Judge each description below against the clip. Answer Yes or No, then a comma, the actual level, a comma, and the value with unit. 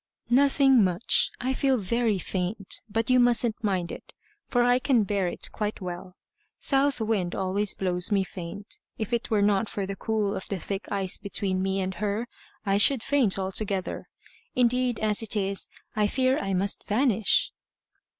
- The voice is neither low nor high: No, high, 205 Hz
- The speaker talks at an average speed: Yes, average, 170 wpm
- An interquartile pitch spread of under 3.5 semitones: No, average, 3.8 semitones